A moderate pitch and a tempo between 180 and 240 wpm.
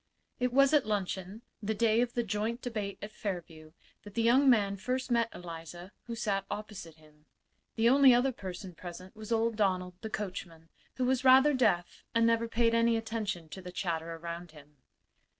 No: high, 210 Hz; average, 185 wpm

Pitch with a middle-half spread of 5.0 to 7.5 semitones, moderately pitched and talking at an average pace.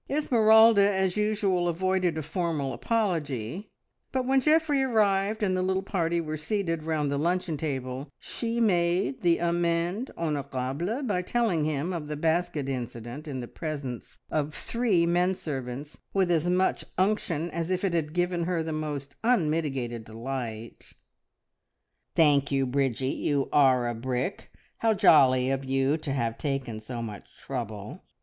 Yes: wide, 5.6 semitones; medium, 165 Hz; average, 150 wpm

